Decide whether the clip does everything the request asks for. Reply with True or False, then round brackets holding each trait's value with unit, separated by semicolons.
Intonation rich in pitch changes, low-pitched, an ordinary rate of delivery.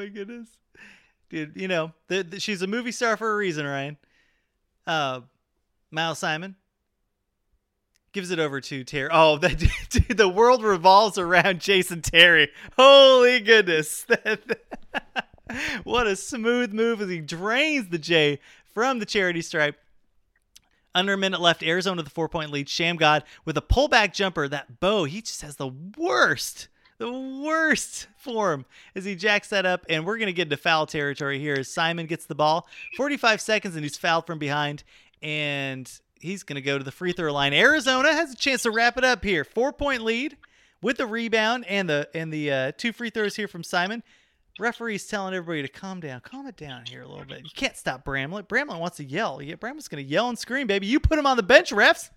False (7.0 semitones; 185 Hz; 195 wpm)